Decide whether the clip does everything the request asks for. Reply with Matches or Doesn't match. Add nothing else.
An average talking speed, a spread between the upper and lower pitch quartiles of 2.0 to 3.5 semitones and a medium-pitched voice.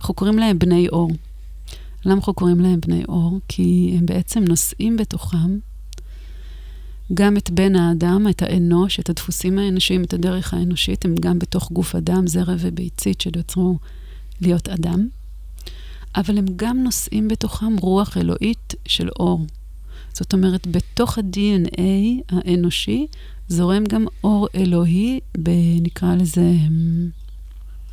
Matches